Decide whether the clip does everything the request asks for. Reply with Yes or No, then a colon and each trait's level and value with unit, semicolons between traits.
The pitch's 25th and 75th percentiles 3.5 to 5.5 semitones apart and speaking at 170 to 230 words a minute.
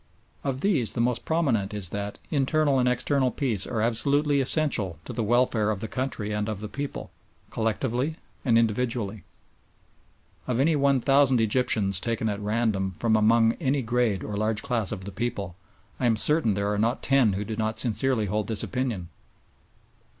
Yes: average, 3.9 semitones; average, 175 wpm